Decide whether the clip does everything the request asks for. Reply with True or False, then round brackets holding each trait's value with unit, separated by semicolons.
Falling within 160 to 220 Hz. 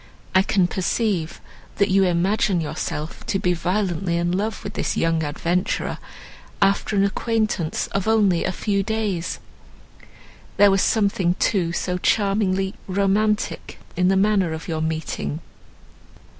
True (190 Hz)